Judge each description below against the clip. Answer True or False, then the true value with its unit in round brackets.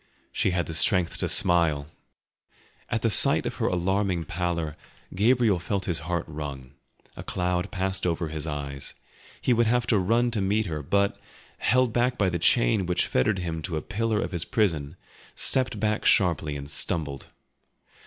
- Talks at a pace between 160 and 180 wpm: True (170 wpm)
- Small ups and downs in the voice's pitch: False (4.6 semitones)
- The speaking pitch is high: False (90 Hz)